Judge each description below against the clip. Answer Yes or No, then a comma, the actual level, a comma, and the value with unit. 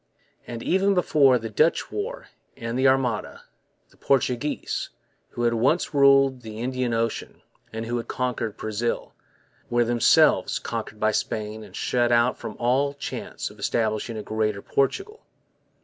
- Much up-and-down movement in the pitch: No, average, 3.4 semitones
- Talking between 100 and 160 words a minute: Yes, average, 150 wpm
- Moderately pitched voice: No, low, 120 Hz